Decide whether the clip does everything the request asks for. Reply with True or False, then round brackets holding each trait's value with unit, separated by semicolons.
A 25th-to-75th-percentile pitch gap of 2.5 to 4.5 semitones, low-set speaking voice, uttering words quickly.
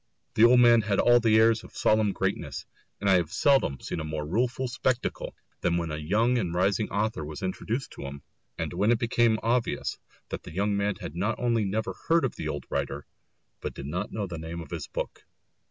False (5.4 semitones; 105 Hz; 220 wpm)